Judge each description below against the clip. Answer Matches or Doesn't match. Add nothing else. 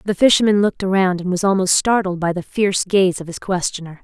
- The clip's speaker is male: Doesn't match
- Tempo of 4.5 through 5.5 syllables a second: Doesn't match